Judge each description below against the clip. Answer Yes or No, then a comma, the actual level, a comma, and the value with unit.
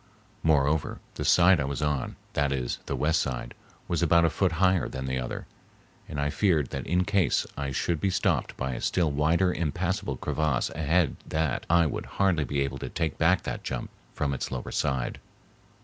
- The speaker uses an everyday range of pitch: Yes, average, 4.0 semitones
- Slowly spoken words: No, average, 185 wpm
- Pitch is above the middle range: No, very low, 75 Hz